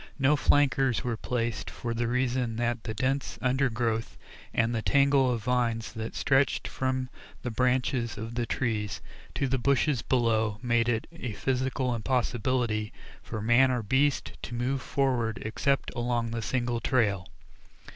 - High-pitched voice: No, low, 120 Hz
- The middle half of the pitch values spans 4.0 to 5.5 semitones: No, narrow, 2.4 semitones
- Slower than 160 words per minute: Yes, average, 150 wpm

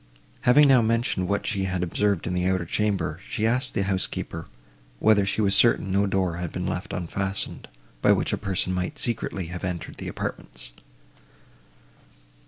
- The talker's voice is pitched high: No, very low, 95 Hz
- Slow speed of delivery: No, average, 170 wpm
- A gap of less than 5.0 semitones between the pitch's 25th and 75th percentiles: Yes, average, 2.8 semitones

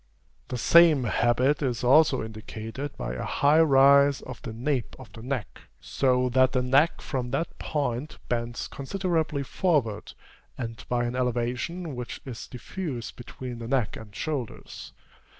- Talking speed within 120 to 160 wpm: Yes, average, 150 wpm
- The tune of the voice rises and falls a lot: No, average, 3.2 semitones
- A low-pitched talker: Yes, low, 130 Hz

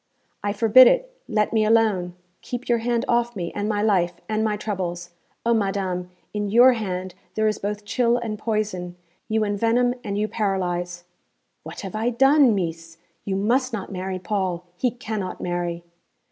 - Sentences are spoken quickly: No, average, 170 wpm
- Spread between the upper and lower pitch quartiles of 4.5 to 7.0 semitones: No, average, 3.7 semitones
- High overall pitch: Yes, high, 210 Hz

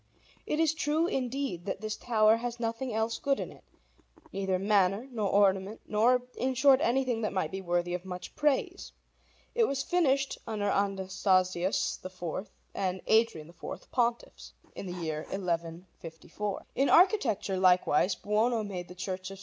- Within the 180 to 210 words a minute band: No, average, 160 wpm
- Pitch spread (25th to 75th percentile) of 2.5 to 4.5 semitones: No, average, 5.1 semitones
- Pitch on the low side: No, high, 205 Hz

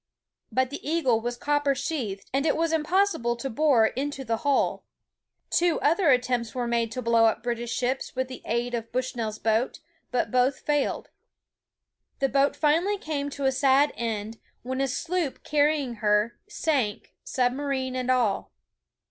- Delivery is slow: No, average, 165 wpm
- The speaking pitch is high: Yes, very high, 260 Hz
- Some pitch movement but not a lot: Yes, average, 3.6 semitones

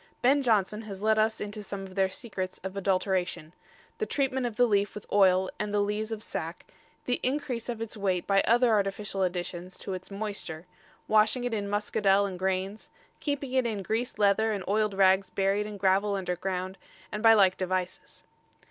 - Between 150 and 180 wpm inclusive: No, average, 190 wpm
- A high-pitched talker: Yes, high, 205 Hz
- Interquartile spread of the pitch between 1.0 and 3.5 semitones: Yes, narrow, 2.4 semitones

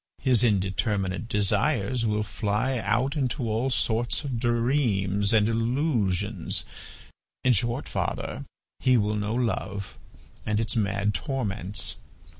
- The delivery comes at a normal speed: No, slow, 115 wpm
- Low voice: Yes, low, 110 Hz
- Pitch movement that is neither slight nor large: Yes, average, 3.4 semitones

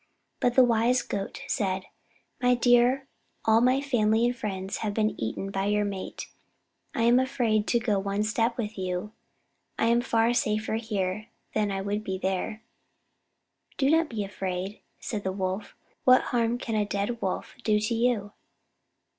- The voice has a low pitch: No, high, 215 Hz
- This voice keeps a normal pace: Yes, average, 165 wpm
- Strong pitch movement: No, average, 3.2 semitones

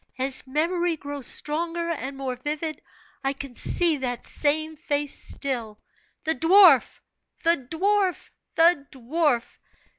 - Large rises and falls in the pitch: No, average, 3.7 semitones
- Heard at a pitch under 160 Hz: No, very high, 295 Hz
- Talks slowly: Yes, slow, 120 wpm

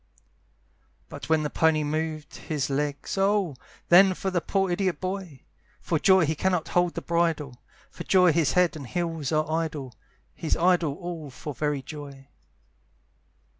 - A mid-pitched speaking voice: Yes, medium, 160 Hz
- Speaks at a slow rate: No, average, 155 wpm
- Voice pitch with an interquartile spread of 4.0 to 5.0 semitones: No, average, 3.2 semitones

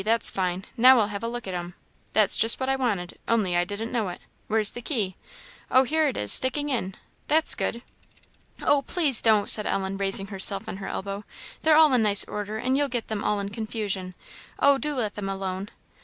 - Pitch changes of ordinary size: Yes, average, 4.6 semitones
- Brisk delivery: Yes, fast, 215 wpm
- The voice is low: No, high, 215 Hz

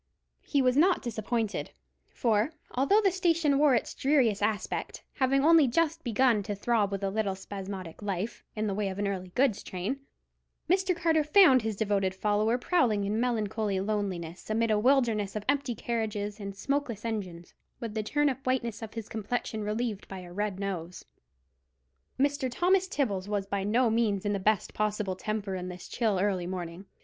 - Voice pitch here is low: No, high, 215 Hz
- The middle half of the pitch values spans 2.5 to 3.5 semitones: No, average, 4.5 semitones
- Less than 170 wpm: No, average, 175 wpm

